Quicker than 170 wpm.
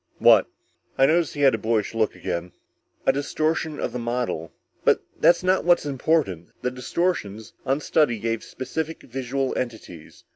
No: average, 155 wpm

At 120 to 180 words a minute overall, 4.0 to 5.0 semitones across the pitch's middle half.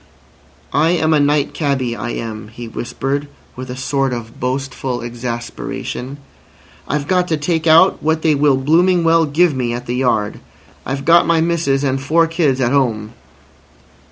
Yes: average, 165 wpm; average, 4.4 semitones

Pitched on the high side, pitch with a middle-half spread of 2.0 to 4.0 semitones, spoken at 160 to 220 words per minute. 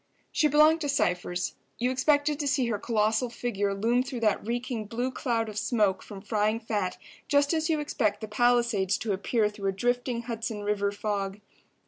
Yes: high, 230 Hz; average, 3.5 semitones; average, 180 wpm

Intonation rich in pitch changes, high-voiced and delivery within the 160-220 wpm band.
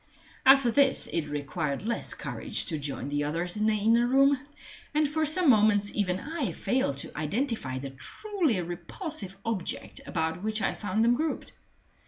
Yes: wide, 8.6 semitones; high, 215 Hz; average, 165 wpm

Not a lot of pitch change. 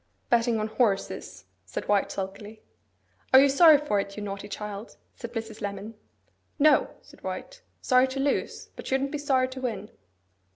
No: average, 4.6 semitones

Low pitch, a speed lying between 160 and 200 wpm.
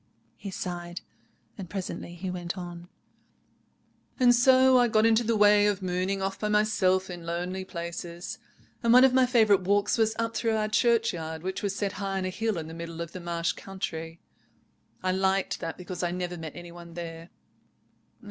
No: medium, 185 Hz; average, 185 wpm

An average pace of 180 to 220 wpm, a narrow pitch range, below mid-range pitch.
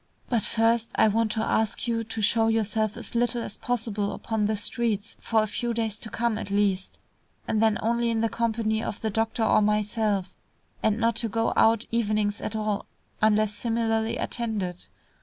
No: average, 185 wpm; narrow, 1.4 semitones; high, 220 Hz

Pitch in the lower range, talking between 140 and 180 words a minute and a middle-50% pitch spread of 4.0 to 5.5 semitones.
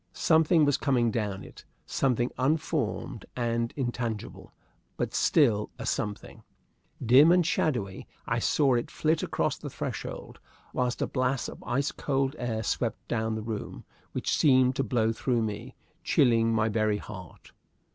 No: low, 120 Hz; average, 145 wpm; average, 3.6 semitones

